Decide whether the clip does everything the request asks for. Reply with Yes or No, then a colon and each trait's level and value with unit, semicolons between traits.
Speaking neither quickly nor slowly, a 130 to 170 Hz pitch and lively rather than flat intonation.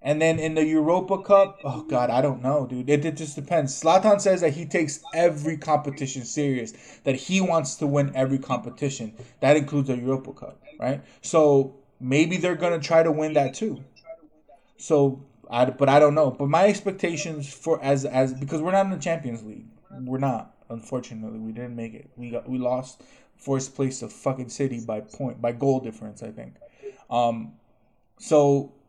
No: average, 185 wpm; medium, 140 Hz; average, 4.1 semitones